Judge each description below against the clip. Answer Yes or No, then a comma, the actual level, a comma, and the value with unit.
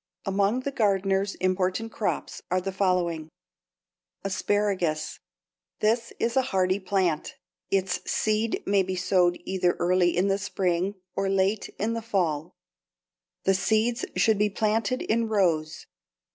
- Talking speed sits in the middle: No, slow, 130 wpm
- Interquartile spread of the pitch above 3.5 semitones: No, average, 2.7 semitones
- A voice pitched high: Yes, high, 195 Hz